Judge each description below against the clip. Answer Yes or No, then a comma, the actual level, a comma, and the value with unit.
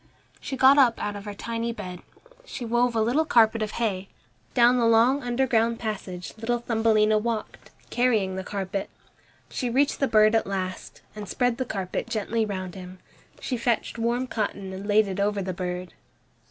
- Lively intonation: No, average, 3.2 semitones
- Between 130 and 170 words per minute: No, average, 180 wpm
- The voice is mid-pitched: No, high, 220 Hz